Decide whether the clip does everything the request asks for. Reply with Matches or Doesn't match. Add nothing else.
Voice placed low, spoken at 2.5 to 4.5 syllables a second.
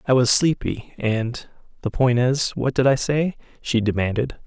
Matches